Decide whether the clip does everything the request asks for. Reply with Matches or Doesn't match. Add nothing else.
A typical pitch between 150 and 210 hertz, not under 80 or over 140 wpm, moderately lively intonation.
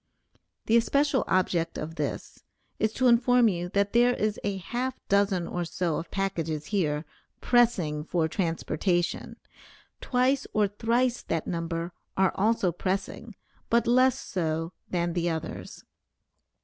Doesn't match